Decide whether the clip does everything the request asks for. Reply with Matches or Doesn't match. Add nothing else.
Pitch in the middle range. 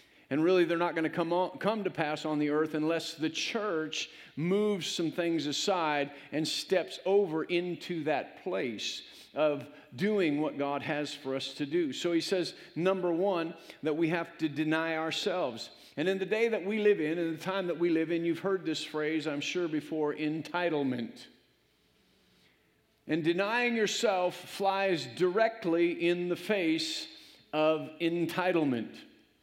Matches